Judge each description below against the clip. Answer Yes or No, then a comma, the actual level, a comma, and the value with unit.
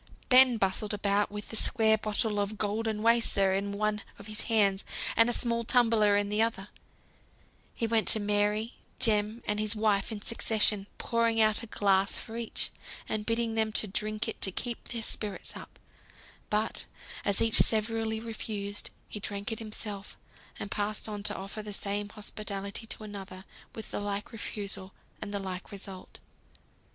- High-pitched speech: Yes, high, 210 Hz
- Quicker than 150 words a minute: Yes, average, 165 wpm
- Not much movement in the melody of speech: Yes, narrow, 1.6 semitones